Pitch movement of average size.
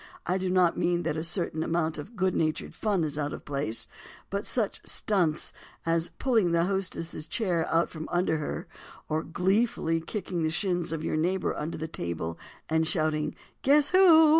Yes: average, 3.3 semitones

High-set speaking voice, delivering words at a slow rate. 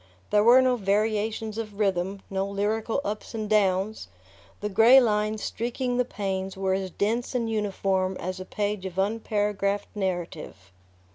No: high, 205 Hz; average, 150 wpm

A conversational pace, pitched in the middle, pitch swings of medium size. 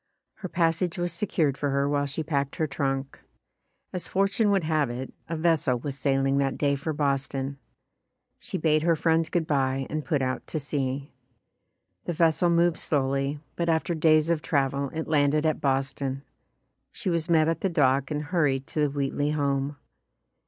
Yes: average, 180 wpm; medium, 145 Hz; average, 3.0 semitones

